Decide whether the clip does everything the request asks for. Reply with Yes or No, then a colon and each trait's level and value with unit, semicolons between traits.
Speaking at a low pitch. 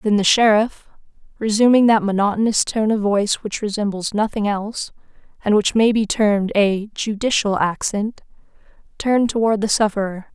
No: high, 210 Hz